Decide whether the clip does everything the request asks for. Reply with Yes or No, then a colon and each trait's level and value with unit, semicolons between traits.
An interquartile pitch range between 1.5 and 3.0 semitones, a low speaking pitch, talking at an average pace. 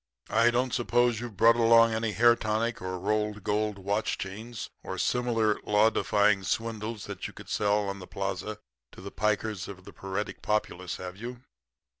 Yes: narrow, 2.6 semitones; low, 105 Hz; average, 175 wpm